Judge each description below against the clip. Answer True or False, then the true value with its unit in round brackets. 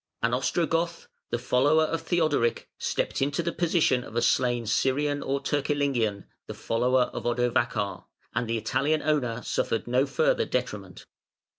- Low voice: True (130 Hz)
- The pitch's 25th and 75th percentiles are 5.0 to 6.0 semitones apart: False (4.3 semitones)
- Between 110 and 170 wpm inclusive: True (145 wpm)